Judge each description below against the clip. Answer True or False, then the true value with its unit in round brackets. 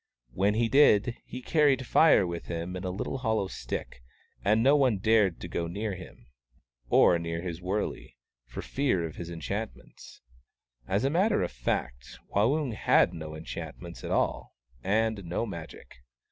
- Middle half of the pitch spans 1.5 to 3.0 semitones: False (5.6 semitones)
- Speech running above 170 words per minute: False (160 wpm)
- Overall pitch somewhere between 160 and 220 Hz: False (100 Hz)